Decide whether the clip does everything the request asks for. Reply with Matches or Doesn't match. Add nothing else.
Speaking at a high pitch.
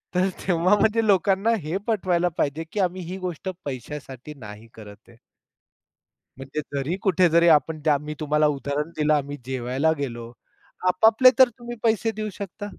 Doesn't match